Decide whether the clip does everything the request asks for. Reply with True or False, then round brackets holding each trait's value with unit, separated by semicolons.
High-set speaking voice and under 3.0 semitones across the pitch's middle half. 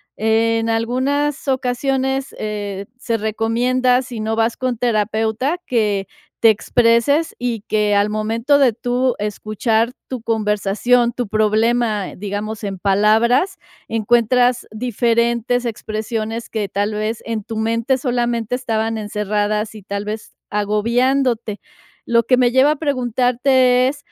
True (230 Hz; 2.6 semitones)